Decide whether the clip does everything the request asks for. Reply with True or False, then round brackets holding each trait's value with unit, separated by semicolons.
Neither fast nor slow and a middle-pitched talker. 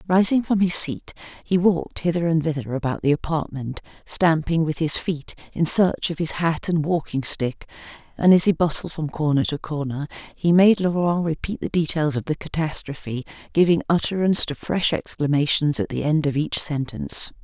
True (180 wpm; 160 Hz)